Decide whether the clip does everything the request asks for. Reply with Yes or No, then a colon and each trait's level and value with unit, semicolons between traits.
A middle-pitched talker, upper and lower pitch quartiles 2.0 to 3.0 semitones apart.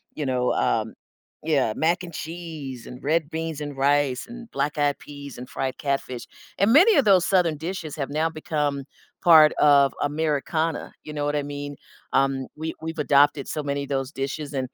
Yes: medium, 145 Hz; average, 2.7 semitones